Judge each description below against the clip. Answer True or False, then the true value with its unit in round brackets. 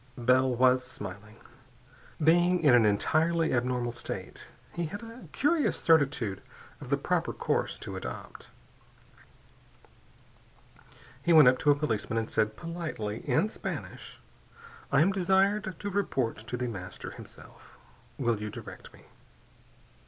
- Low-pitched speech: True (130 Hz)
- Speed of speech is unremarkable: False (130 wpm)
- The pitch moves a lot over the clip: True (7.1 semitones)